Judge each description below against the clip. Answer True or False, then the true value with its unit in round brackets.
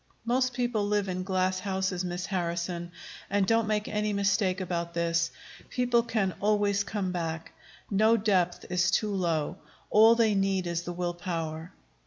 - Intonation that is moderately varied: True (3.1 semitones)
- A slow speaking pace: False (155 wpm)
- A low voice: False (190 Hz)